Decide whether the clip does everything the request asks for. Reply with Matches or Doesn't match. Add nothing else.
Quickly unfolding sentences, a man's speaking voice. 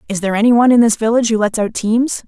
Doesn't match